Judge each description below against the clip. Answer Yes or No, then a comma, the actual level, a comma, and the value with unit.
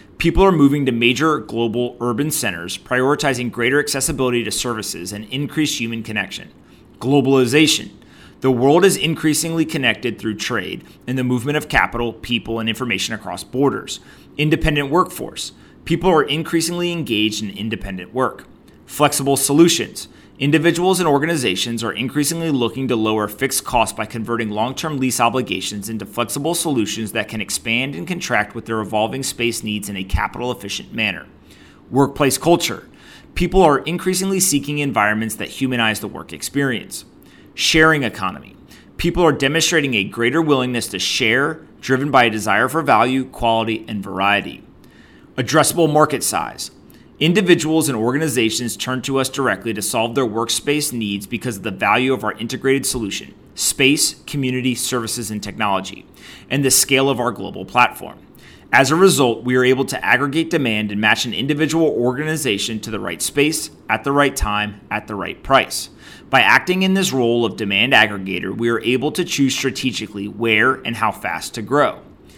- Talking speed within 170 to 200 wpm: No, average, 160 wpm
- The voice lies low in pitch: Yes, low, 125 Hz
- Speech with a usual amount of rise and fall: Yes, average, 4.8 semitones